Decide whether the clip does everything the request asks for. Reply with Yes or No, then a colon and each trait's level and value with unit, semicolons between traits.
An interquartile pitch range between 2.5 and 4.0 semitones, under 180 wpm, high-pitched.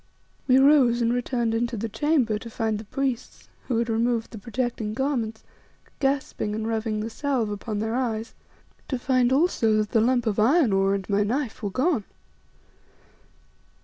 Yes: average, 3.1 semitones; average, 170 wpm; high, 230 Hz